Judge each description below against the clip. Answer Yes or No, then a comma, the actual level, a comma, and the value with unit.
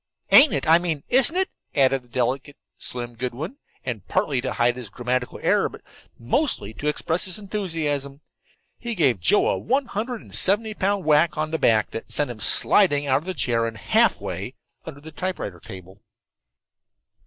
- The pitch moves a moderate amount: No, wide, 7.4 semitones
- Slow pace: No, average, 180 wpm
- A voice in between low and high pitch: Yes, medium, 145 Hz